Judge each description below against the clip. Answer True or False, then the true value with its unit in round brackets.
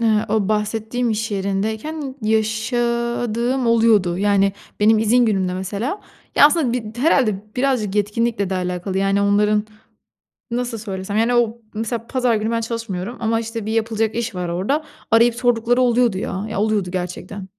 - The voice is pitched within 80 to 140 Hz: False (220 Hz)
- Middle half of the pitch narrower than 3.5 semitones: True (2.8 semitones)